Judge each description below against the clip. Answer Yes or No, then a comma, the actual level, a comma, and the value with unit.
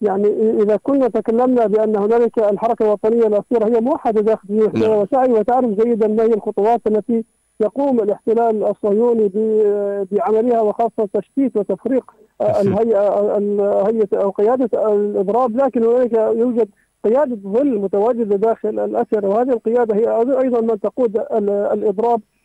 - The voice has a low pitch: No, high, 220 Hz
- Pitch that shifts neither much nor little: No, narrow, 2.1 semitones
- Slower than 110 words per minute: No, average, 125 wpm